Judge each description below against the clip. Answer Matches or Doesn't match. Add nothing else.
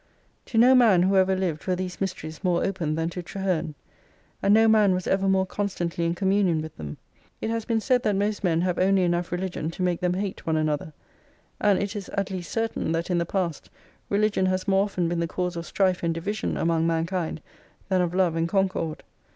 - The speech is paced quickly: Matches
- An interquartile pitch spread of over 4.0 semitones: Doesn't match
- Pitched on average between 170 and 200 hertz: Matches